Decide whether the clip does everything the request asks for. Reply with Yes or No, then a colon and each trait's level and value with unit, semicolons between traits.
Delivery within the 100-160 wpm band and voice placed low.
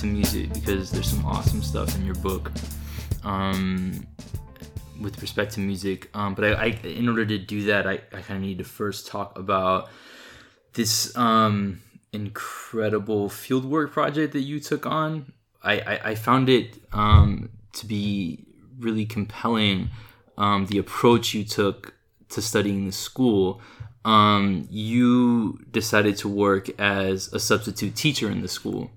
Yes: average, 145 wpm; low, 105 Hz